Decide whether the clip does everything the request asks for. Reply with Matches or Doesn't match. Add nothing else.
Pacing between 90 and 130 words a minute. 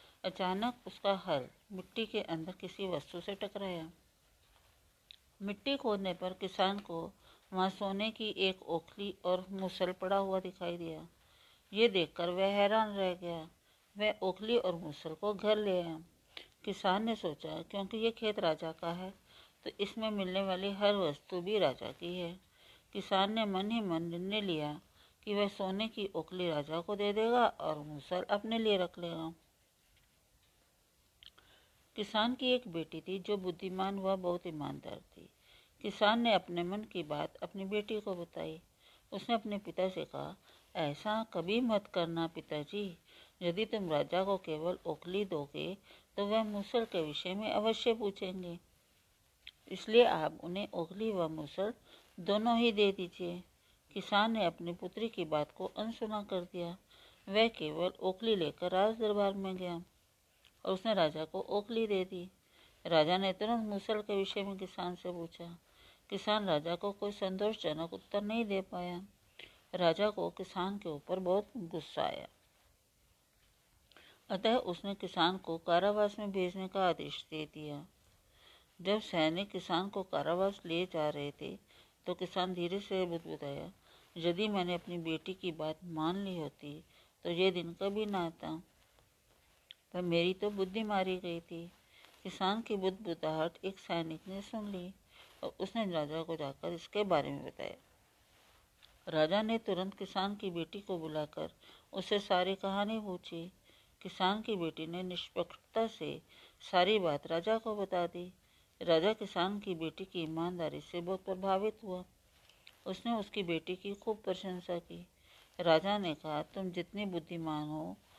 Doesn't match